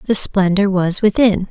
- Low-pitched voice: No, high, 195 Hz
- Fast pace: No, average, 160 wpm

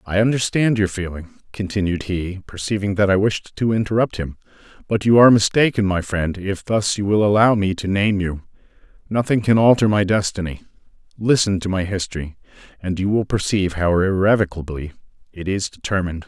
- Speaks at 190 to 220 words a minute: No, average, 170 wpm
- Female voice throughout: No, male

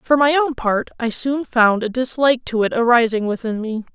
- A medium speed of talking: No, fast, 215 wpm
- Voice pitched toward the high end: Yes, high, 240 Hz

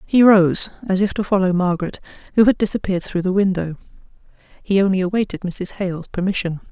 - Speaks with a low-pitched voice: No, high, 190 Hz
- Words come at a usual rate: Yes, average, 170 wpm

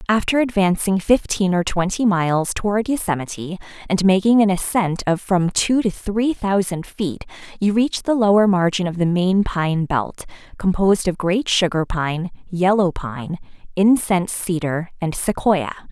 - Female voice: Yes, female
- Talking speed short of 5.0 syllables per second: Yes, 4.5 syllables/s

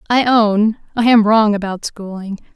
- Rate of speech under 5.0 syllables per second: Yes, 4.3 syllables/s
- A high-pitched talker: Yes, high, 215 Hz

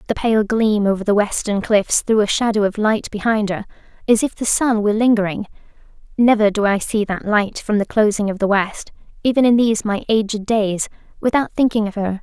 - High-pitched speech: Yes, high, 210 Hz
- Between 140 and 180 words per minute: No, fast, 205 wpm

